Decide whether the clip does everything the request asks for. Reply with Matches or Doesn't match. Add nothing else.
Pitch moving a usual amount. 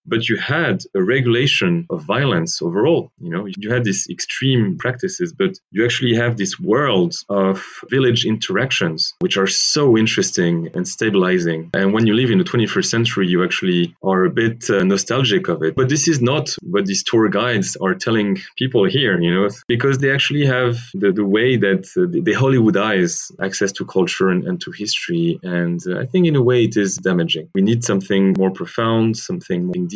Doesn't match